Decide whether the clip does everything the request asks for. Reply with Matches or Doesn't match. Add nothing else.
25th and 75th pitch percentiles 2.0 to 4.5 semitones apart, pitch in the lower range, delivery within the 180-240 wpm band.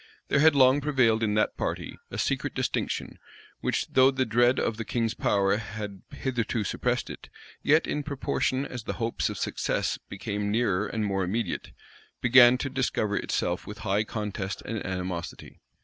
Doesn't match